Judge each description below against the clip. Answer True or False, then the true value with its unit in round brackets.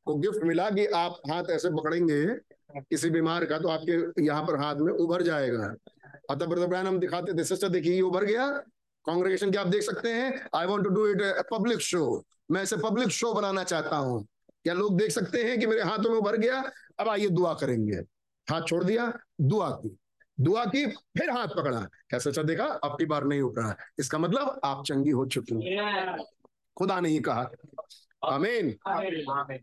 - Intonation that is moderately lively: False (5.7 semitones)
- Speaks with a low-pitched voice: False (175 Hz)